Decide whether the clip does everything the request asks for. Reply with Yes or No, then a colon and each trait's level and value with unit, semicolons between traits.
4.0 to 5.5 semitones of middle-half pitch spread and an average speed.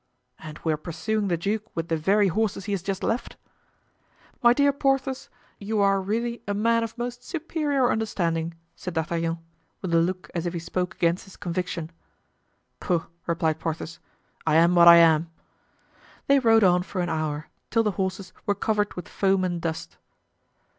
Yes: average, 4.6 semitones; average, 175 wpm